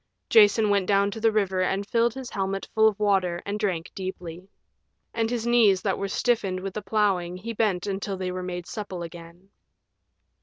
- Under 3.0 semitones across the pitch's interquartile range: Yes, narrow, 2.6 semitones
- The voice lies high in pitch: Yes, high, 195 Hz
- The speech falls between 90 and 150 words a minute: No, average, 190 wpm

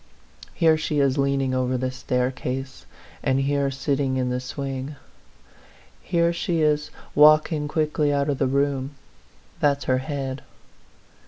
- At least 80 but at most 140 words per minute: Yes, slow, 135 wpm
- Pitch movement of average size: No, narrow, 2.2 semitones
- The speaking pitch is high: No, medium, 140 Hz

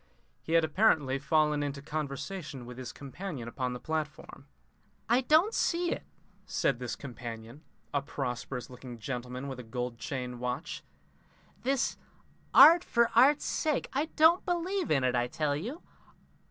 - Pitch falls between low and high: Yes, medium, 145 Hz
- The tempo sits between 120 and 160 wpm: Yes, average, 150 wpm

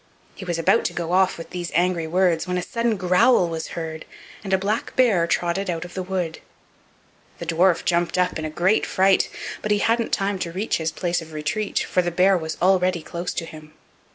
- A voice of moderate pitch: Yes, medium, 180 Hz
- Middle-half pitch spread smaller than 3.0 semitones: Yes, narrow, 2.4 semitones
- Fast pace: Yes, fast, 210 wpm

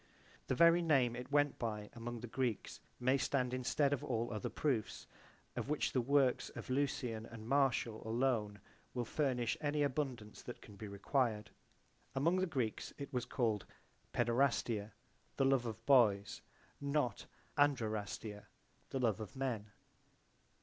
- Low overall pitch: Yes, low, 125 Hz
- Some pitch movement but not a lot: Yes, average, 3.8 semitones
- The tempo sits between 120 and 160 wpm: Yes, average, 145 wpm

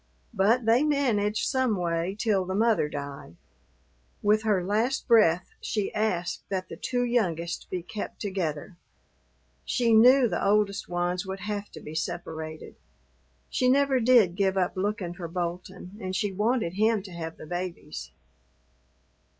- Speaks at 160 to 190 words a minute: No, average, 150 wpm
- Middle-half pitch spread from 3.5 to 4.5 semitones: Yes, average, 4.0 semitones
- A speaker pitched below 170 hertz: No, high, 195 Hz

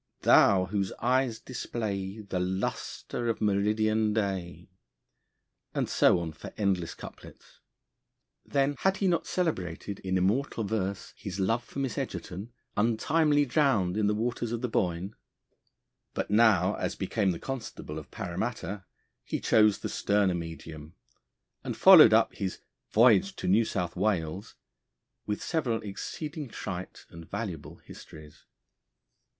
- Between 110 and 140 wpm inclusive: Yes, slow, 135 wpm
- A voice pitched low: Yes, low, 105 Hz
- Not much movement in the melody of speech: No, average, 4.3 semitones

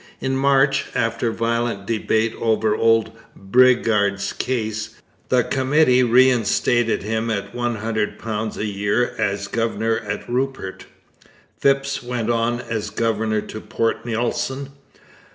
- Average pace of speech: No, slow, 110 wpm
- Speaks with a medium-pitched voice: No, low, 115 Hz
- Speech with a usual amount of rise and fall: No, narrow, 2.2 semitones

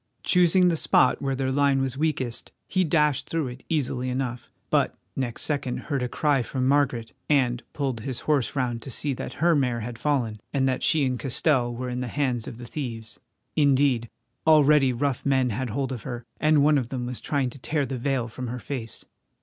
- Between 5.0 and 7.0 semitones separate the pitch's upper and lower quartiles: No, average, 2.8 semitones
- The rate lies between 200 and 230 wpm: Yes, fast, 205 wpm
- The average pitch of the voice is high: No, low, 130 Hz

